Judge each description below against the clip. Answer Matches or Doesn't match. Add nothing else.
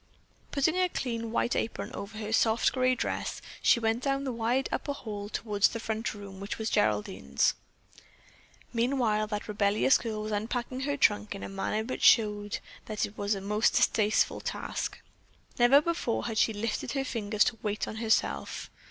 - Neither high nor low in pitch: Doesn't match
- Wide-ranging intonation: Doesn't match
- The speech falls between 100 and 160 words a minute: Doesn't match